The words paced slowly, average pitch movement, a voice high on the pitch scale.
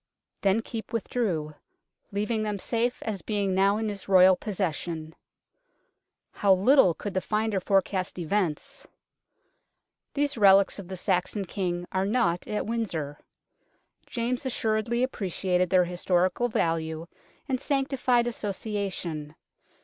Yes: slow, 125 wpm; average, 3.9 semitones; high, 200 Hz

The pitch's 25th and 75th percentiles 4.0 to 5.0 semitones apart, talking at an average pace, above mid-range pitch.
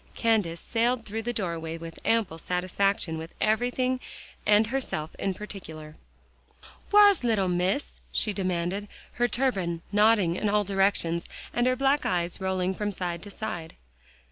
Yes: average, 4.7 semitones; average, 145 wpm; high, 200 Hz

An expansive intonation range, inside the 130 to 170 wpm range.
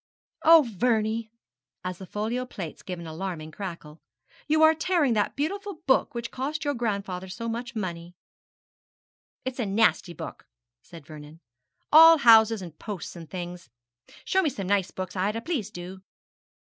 Yes: wide, 6.2 semitones; average, 155 wpm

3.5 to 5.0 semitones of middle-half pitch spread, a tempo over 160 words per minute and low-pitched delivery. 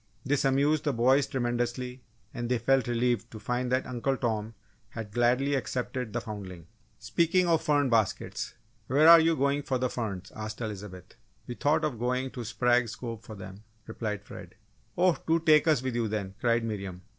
Yes: average, 3.8 semitones; average, 180 wpm; low, 120 Hz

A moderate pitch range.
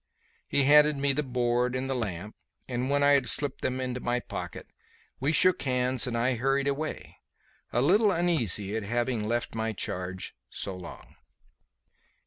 Yes: average, 3.3 semitones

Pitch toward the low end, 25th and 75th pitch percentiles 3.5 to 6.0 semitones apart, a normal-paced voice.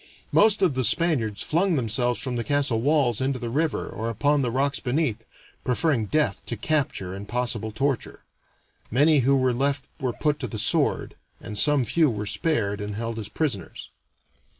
Yes: low, 125 Hz; average, 4.5 semitones; average, 175 wpm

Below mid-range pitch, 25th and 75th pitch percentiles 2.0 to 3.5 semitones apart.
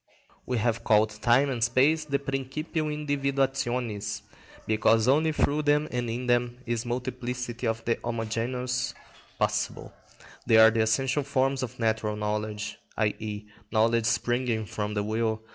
Yes: low, 120 Hz; average, 3.2 semitones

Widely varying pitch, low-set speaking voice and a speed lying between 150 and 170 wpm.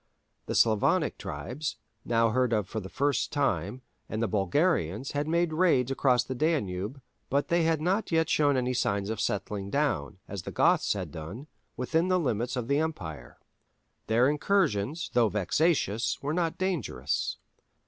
Yes: wide, 6.7 semitones; low, 125 Hz; average, 155 wpm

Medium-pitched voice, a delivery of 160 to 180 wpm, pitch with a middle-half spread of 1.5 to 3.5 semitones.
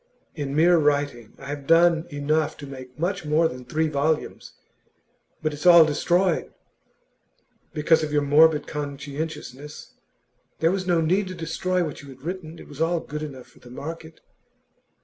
Yes: medium, 155 Hz; average, 165 wpm; narrow, 2.5 semitones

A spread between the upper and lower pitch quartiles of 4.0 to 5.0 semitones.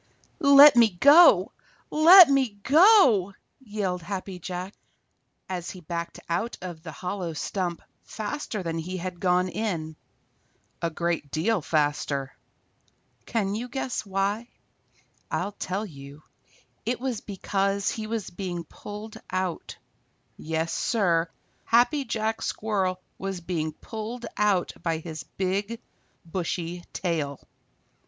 Yes: average, 4.5 semitones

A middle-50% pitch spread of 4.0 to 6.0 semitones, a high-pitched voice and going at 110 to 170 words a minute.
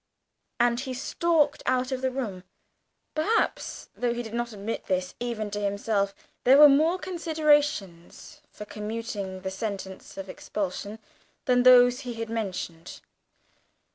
Yes: average, 4.7 semitones; high, 235 Hz; average, 140 wpm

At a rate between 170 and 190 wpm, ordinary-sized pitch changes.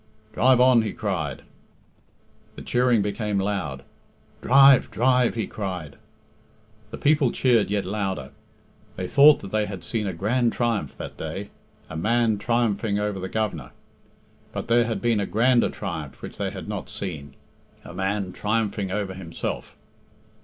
No: average, 150 wpm; average, 3.8 semitones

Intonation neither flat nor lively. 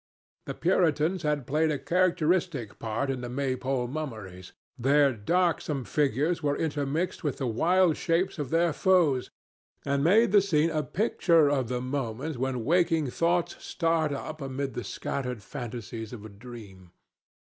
Yes: average, 5.0 semitones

